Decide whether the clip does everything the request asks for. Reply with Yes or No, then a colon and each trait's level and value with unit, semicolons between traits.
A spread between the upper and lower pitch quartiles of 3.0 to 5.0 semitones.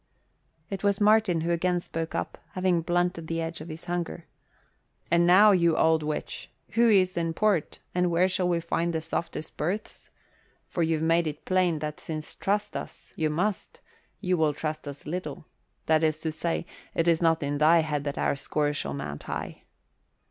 No: narrow, 2.5 semitones